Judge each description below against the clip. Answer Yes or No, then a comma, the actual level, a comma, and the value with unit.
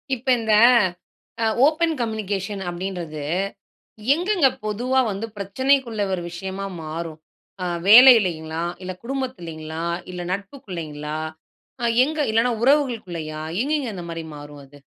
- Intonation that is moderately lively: No, wide, 7.2 semitones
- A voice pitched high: Yes, high, 195 Hz